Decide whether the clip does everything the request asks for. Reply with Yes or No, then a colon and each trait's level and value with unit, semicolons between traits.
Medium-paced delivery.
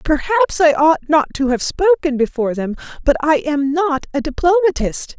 Yes: average, 175 wpm